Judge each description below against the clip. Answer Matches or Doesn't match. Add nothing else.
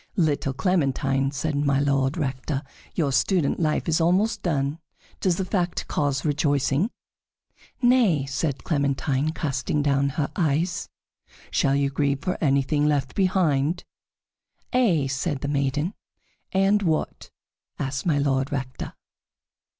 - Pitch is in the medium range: Matches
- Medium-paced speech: Doesn't match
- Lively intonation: Doesn't match